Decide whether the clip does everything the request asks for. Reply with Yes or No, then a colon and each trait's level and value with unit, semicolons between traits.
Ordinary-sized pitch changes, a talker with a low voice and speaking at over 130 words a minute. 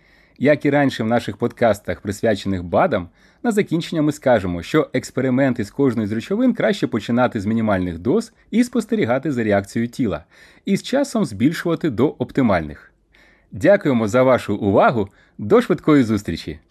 No: wide, 7.9 semitones; low, 130 Hz; average, 145 wpm